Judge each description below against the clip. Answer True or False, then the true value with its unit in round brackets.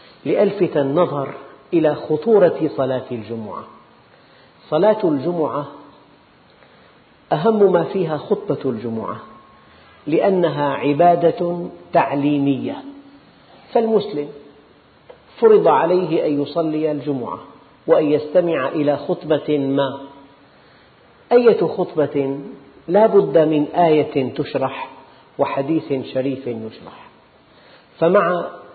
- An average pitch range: True (4.1 semitones)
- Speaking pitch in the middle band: True (155 Hz)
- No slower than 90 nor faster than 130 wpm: False (80 wpm)